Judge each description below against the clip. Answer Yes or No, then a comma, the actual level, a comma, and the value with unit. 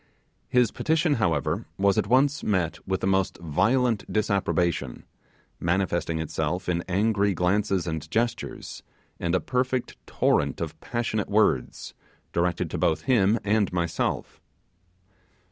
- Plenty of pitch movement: No, average, 4.6 semitones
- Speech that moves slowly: Yes, slow, 125 wpm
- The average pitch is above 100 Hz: No, very low, 95 Hz